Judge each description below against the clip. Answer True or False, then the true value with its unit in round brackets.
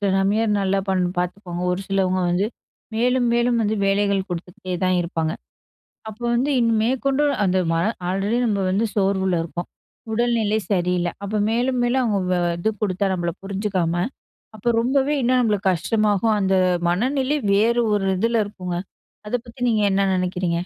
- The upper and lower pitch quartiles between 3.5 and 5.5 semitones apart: True (4.1 semitones)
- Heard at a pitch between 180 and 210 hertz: True (200 Hz)